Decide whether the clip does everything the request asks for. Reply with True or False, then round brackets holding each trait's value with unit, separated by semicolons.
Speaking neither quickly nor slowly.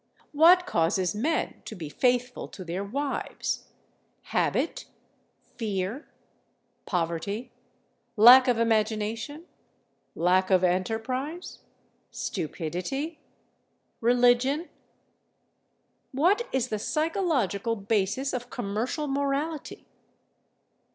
False (80 wpm)